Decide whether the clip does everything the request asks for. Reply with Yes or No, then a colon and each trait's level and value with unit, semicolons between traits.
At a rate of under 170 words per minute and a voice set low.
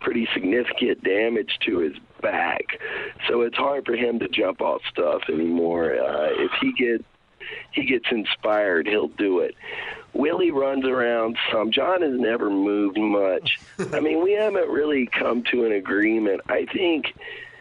No: average, 155 wpm; high, 220 Hz